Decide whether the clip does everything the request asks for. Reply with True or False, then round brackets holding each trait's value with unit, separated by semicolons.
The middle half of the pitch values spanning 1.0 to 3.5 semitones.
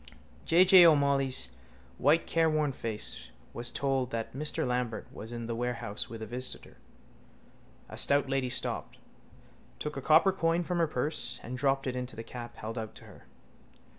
False (4.1 semitones)